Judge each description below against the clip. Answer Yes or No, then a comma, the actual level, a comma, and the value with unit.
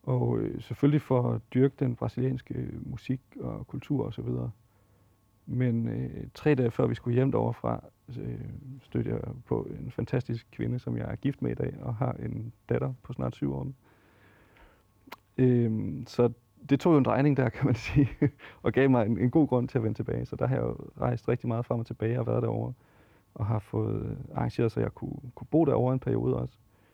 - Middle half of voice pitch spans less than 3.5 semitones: Yes, average, 3.0 semitones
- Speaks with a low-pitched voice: Yes, low, 120 Hz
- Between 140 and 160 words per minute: No, average, 205 wpm